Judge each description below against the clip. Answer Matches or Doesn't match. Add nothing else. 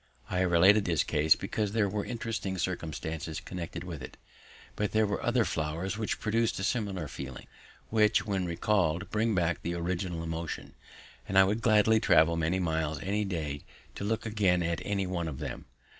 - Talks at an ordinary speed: Matches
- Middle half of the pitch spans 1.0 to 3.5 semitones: Doesn't match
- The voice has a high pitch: Doesn't match